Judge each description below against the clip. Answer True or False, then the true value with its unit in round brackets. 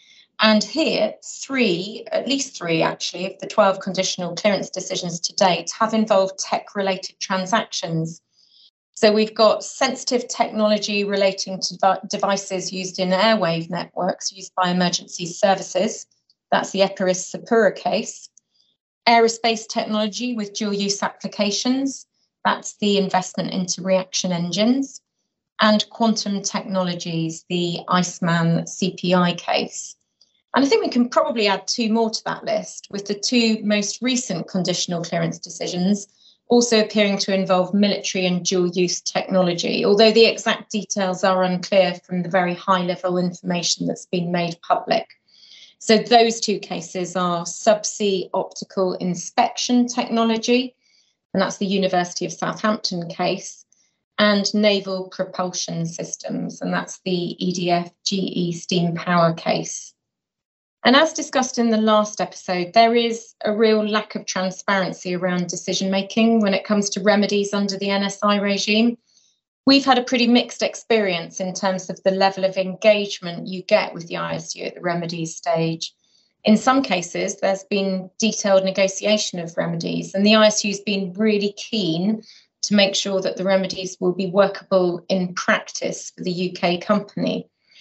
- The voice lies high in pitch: True (195 Hz)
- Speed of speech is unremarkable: True (145 wpm)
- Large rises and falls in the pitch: False (2.9 semitones)